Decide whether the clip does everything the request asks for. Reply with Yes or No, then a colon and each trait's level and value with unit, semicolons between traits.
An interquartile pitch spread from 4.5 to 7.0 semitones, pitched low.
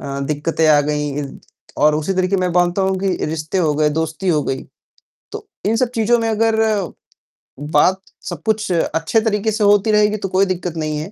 No: average, 5.3 semitones; medium, 185 Hz